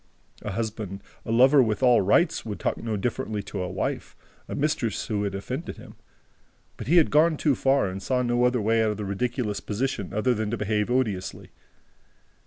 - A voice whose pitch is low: Yes, low, 115 Hz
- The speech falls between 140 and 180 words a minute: No, average, 195 wpm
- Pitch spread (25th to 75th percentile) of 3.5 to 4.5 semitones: Yes, average, 3.9 semitones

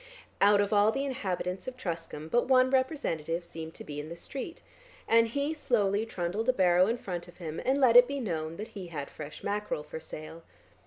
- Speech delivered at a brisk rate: Yes, fast, 210 wpm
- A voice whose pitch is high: Yes, high, 200 Hz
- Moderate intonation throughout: No, wide, 6.8 semitones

